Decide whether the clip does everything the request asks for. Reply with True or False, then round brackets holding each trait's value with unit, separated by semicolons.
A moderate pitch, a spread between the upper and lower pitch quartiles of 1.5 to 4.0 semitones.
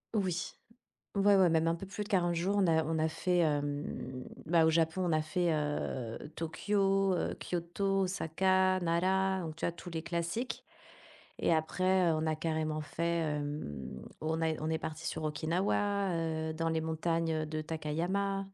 True (165 Hz; 3.0 semitones)